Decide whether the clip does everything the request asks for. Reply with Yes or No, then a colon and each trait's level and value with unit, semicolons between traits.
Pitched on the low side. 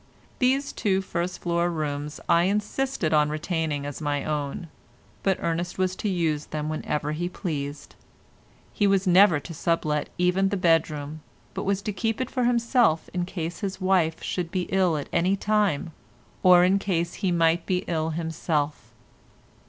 No: medium, 175 Hz